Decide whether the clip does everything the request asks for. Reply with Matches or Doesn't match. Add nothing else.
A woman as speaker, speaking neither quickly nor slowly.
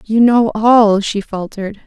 Matches